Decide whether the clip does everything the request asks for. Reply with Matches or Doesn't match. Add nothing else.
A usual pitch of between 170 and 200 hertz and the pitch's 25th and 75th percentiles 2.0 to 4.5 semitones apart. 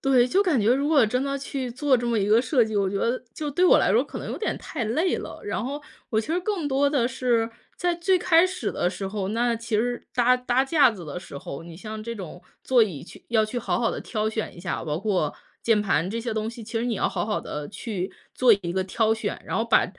Doesn't match